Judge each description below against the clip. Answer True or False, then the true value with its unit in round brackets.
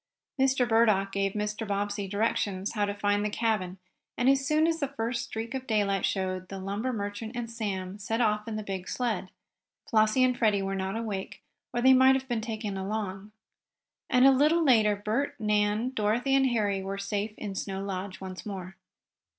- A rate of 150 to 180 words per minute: False (190 wpm)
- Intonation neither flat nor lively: True (3.4 semitones)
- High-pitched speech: True (210 Hz)